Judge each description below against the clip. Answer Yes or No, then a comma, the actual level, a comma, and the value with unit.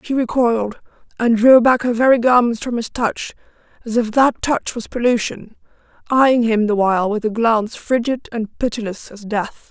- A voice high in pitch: Yes, high, 230 Hz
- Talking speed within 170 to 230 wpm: Yes, average, 180 wpm